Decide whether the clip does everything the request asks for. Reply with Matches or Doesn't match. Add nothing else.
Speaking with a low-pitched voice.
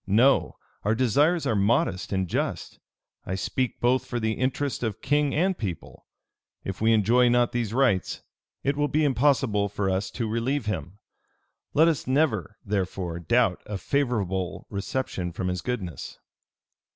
Matches